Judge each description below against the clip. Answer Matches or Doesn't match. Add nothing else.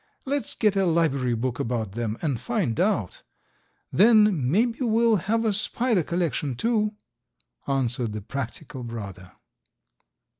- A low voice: Doesn't match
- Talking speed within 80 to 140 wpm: Matches